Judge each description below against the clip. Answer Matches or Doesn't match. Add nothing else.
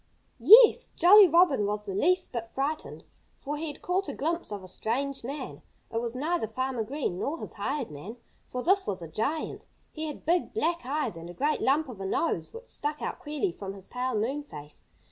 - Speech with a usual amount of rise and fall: Doesn't match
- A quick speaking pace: Matches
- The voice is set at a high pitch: Matches